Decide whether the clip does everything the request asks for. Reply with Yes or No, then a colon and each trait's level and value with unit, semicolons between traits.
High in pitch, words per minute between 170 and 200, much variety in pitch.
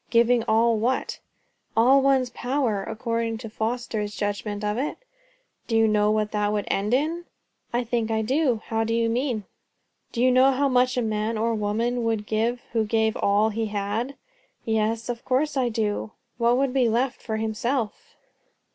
No: high, 230 Hz; average, 180 wpm; narrow, 2.5 semitones